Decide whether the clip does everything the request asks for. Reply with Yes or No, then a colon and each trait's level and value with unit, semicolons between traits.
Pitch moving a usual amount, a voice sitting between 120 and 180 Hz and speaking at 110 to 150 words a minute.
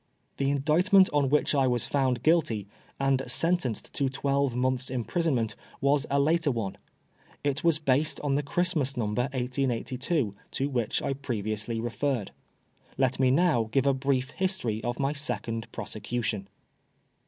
Yes: average, 3.2 semitones; low, 135 Hz; average, 145 wpm